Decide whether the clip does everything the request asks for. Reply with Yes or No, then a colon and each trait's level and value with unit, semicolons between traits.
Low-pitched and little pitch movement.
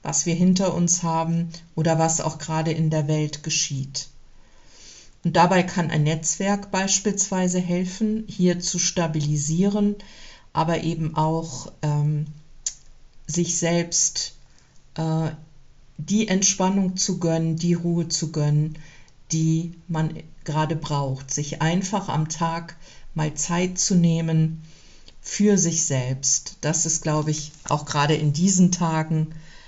No: medium, 160 Hz; narrow, 2.3 semitones